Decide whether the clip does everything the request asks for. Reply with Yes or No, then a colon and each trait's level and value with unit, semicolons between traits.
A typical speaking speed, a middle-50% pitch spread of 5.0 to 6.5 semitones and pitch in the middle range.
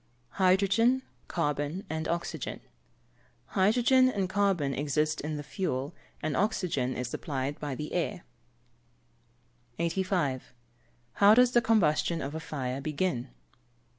No: slow, 120 wpm; average, 5.3 semitones; medium, 165 Hz